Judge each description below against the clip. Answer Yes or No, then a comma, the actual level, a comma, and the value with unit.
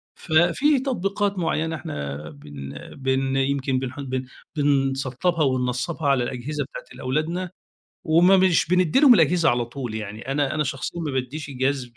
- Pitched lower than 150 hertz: Yes, medium, 140 Hz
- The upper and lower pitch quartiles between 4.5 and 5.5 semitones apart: Yes, average, 4.8 semitones